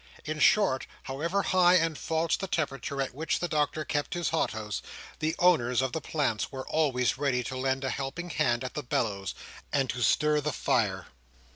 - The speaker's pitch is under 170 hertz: Yes, medium, 140 Hz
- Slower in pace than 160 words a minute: No, average, 185 wpm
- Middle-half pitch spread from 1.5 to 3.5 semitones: No, average, 4.0 semitones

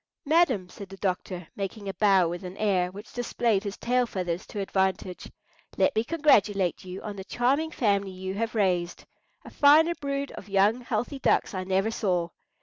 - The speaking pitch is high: Yes, high, 200 Hz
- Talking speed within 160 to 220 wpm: Yes, average, 180 wpm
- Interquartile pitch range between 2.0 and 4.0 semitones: No, average, 4.4 semitones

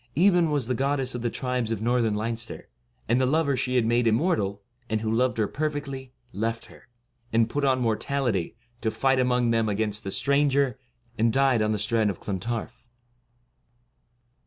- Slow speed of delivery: No, average, 175 wpm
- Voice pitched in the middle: No, low, 120 Hz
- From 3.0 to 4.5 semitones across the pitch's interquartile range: Yes, average, 3.3 semitones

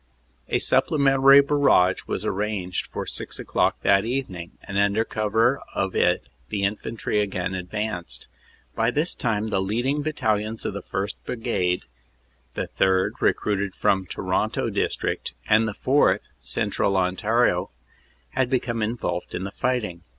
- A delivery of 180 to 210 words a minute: No, average, 140 wpm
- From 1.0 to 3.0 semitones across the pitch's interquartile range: No, average, 4.0 semitones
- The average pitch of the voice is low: Yes, low, 105 Hz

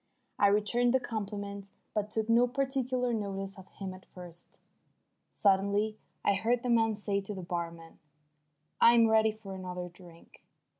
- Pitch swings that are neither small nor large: Yes, average, 3.1 semitones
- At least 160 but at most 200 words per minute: No, average, 150 wpm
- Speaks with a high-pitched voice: Yes, high, 205 Hz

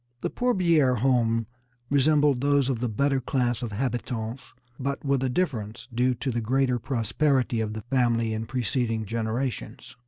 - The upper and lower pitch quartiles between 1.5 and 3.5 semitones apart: Yes, average, 3.1 semitones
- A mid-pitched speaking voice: No, low, 125 Hz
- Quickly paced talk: No, average, 155 wpm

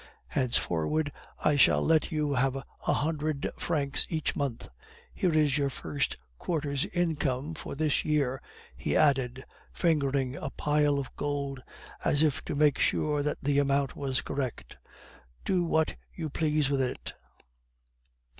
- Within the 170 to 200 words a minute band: No, average, 140 wpm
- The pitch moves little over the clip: Yes, narrow, 2.1 semitones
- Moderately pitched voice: Yes, medium, 145 Hz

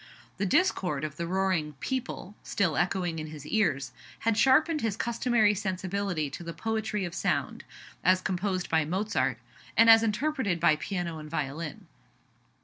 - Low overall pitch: No, medium, 185 Hz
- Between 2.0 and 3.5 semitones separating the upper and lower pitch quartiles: No, average, 5.2 semitones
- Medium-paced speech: Yes, average, 150 wpm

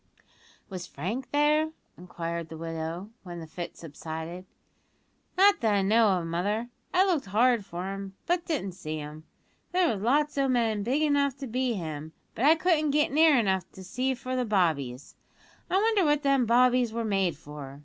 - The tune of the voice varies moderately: No, wide, 8.2 semitones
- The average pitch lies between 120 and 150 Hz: No, high, 215 Hz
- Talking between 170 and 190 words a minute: Yes, average, 180 wpm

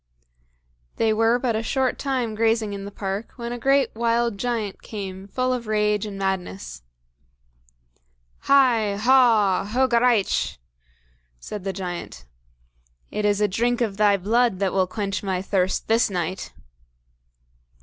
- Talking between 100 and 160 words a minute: Yes, average, 140 wpm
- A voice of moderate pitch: No, high, 215 Hz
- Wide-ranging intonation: No, average, 3.4 semitones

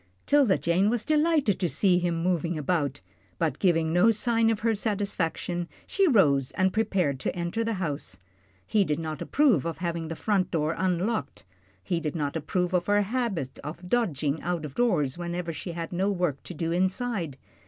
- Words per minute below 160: No, average, 185 wpm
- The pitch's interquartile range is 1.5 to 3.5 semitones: No, average, 4.2 semitones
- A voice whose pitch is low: No, medium, 175 Hz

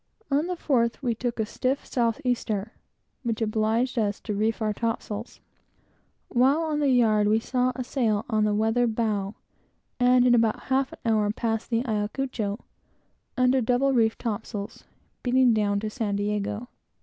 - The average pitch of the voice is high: Yes, high, 230 Hz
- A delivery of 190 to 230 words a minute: No, average, 160 wpm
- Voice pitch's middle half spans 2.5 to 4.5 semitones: Yes, average, 2.8 semitones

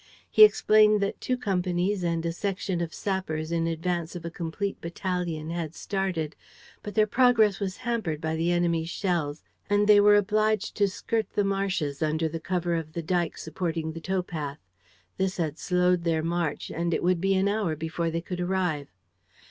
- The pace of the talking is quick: No, average, 180 wpm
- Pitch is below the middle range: No, medium, 175 Hz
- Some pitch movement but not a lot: Yes, average, 3.3 semitones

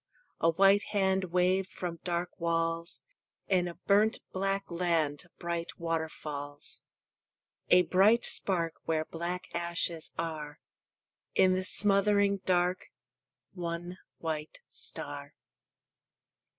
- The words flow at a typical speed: No, slow, 100 wpm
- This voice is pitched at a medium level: Yes, medium, 175 Hz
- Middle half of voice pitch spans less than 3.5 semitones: Yes, narrow, 2.4 semitones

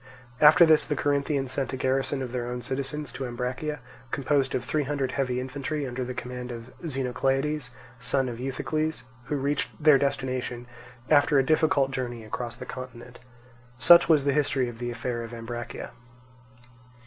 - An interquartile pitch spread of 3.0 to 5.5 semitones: No, narrow, 2.6 semitones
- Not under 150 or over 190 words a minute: Yes, average, 165 wpm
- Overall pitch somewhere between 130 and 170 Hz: Yes, low, 135 Hz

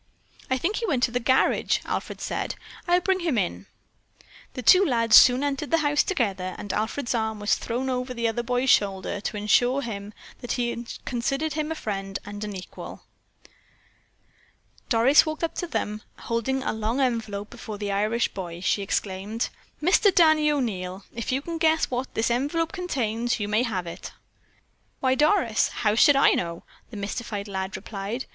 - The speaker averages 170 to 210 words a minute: Yes, average, 180 wpm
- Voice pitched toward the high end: Yes, high, 235 Hz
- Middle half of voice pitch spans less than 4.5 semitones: No, average, 5.2 semitones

